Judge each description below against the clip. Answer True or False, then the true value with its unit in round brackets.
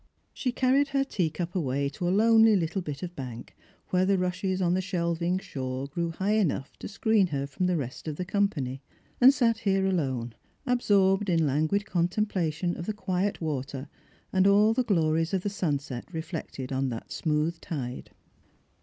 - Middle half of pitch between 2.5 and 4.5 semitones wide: False (5.1 semitones)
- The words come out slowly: False (175 wpm)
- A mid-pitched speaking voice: True (175 Hz)